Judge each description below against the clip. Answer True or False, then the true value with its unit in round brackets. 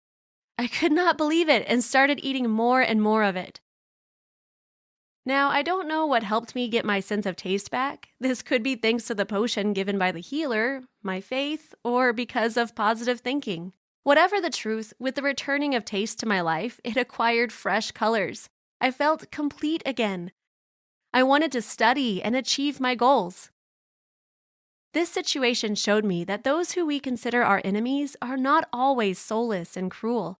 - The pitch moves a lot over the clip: False (4.7 semitones)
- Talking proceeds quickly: False (175 wpm)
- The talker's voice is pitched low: False (240 Hz)